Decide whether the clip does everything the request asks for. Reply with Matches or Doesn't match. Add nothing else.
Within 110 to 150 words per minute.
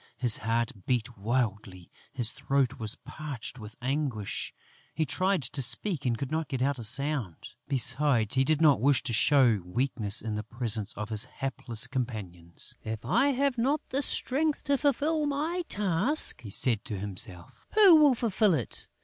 Doesn't match